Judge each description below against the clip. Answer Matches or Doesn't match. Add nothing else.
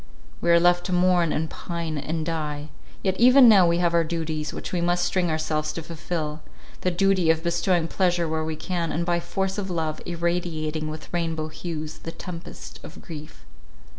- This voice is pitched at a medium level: Matches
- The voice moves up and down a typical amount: Doesn't match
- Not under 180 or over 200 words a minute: Matches